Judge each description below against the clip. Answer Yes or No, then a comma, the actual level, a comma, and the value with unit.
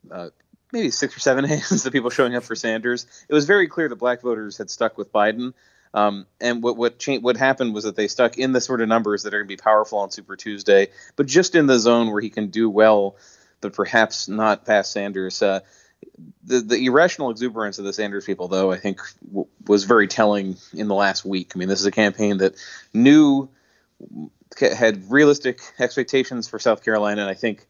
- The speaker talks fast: Yes, fast, 215 wpm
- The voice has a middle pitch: No, low, 110 Hz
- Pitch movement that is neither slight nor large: Yes, average, 3.5 semitones